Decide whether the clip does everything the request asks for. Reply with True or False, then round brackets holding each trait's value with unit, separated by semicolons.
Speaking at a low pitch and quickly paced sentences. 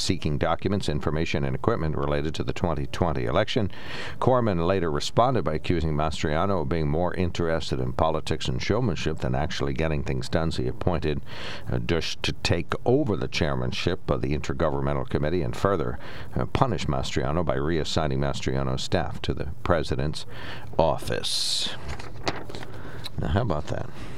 False (80 Hz; 145 wpm)